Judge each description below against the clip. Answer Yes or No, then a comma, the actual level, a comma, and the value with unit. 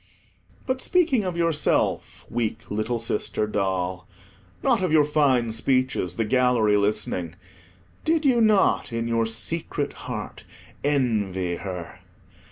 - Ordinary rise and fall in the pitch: No, wide, 7.2 semitones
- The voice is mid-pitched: No, low, 115 Hz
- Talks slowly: Yes, slow, 120 wpm